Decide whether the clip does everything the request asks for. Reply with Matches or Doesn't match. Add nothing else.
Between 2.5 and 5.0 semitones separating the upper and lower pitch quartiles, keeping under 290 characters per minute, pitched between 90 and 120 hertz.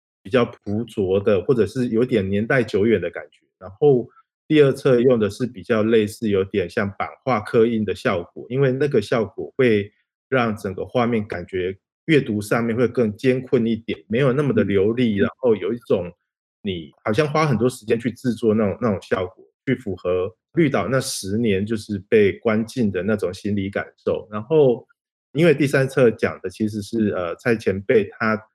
Matches